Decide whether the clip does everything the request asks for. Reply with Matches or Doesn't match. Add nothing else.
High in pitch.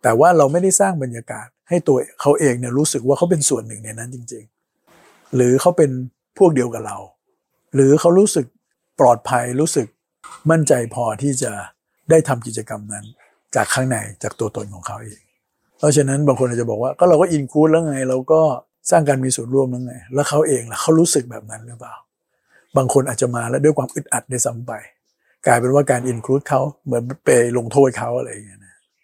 Doesn't match